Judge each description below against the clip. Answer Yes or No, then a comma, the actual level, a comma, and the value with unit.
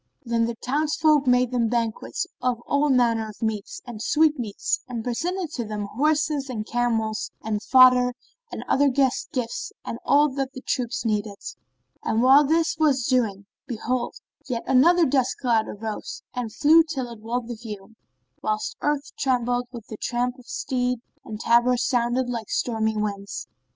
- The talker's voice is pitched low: No, high, 245 Hz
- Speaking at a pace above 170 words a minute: No, average, 165 wpm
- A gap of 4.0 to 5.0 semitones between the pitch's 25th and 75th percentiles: No, average, 3.3 semitones